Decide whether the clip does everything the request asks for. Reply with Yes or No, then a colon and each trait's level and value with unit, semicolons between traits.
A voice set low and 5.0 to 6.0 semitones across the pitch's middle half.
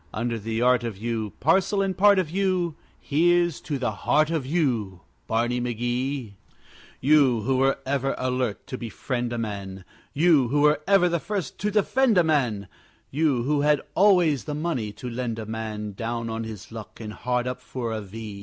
Yes: low, 125 Hz; wide, 5.6 semitones